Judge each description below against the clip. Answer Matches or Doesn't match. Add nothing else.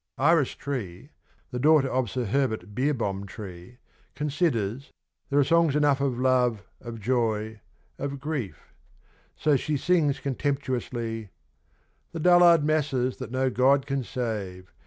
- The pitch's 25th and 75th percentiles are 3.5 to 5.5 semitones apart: Matches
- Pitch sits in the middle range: Doesn't match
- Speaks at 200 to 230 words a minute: Doesn't match